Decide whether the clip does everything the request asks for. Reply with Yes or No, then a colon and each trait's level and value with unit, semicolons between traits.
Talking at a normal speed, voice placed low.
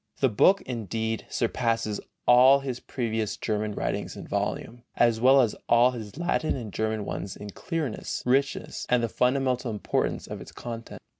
Yes: average, 160 wpm; low, 120 Hz